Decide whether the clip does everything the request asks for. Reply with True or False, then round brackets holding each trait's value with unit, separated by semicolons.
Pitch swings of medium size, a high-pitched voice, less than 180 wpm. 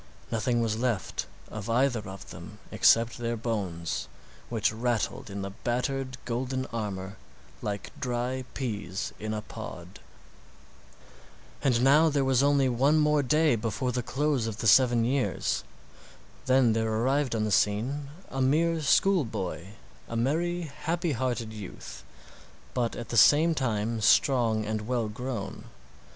False (3.7 semitones; 120 Hz; 140 wpm)